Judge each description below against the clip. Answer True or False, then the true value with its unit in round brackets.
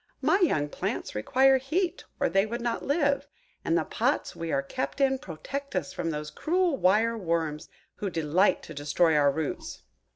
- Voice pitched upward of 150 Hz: True (190 Hz)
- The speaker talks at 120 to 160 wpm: False (175 wpm)